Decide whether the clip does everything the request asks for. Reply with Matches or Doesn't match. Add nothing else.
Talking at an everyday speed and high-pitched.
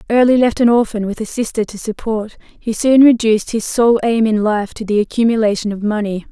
Doesn't match